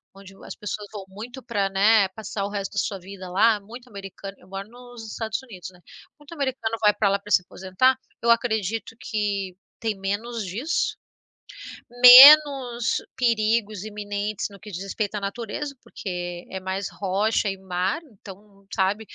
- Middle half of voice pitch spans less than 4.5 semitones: Yes, average, 2.9 semitones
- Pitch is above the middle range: Yes, high, 205 Hz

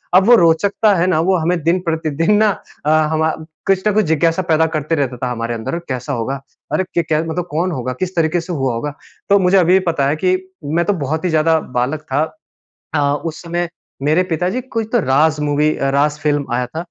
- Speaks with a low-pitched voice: No, medium, 160 Hz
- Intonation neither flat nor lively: Yes, average, 3.6 semitones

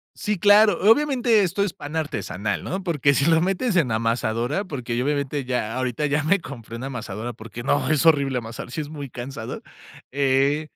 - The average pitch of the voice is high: No, medium, 140 Hz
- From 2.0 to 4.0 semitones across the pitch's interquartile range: No, wide, 5.4 semitones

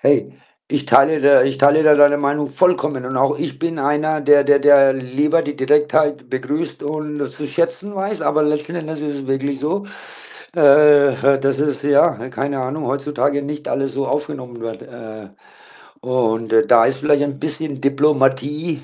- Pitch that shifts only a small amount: Yes, narrow, 1.8 semitones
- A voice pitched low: No, medium, 145 Hz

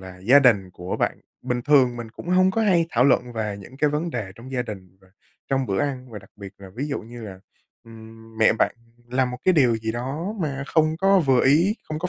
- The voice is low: Yes, low, 125 Hz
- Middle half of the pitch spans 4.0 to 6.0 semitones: Yes, average, 5.1 semitones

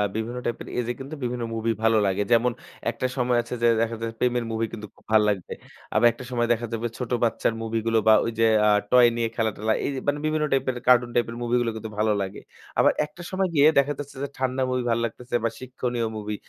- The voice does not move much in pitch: Yes, narrow, 1.9 semitones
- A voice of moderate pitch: No, low, 120 Hz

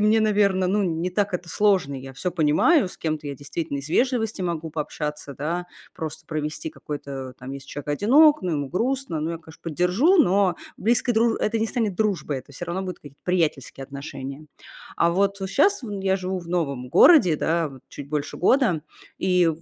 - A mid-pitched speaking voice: Yes, medium, 175 Hz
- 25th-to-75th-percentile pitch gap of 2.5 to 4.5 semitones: No, wide, 5.5 semitones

